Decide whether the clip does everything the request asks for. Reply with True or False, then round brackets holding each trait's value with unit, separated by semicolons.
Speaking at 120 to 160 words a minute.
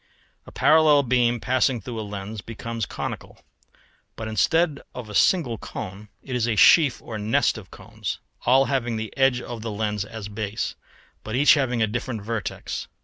False (180 wpm)